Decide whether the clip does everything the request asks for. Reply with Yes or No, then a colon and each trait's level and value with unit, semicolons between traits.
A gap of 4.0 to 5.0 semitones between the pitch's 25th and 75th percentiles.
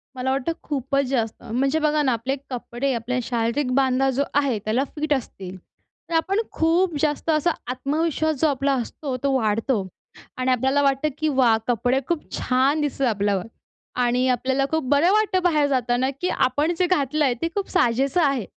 No: average, 3.4 semitones